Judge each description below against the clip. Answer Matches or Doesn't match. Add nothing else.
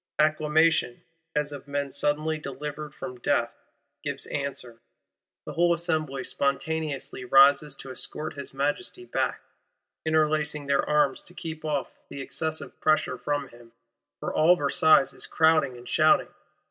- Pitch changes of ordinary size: Doesn't match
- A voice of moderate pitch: Matches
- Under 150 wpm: Matches